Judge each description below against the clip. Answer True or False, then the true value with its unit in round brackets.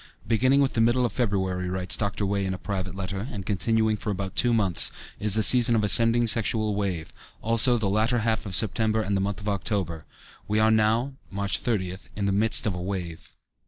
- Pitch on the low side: True (105 Hz)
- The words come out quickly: True (210 wpm)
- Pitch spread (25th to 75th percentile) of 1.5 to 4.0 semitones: True (2.8 semitones)